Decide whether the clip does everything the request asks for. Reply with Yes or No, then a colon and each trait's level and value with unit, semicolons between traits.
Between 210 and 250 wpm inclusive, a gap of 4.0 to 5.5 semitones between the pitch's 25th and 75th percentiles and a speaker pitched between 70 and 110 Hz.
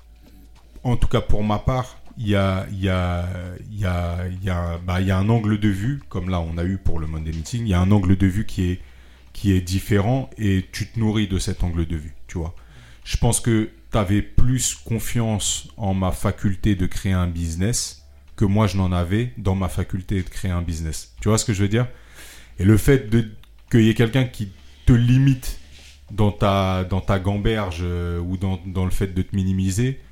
No: fast, 220 wpm; average, 3.6 semitones; very low, 95 Hz